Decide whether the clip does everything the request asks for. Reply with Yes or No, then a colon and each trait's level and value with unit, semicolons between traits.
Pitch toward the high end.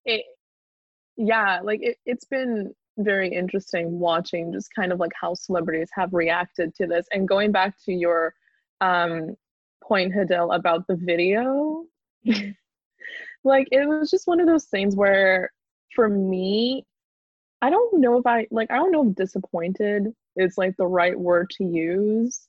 Yes: high, 200 Hz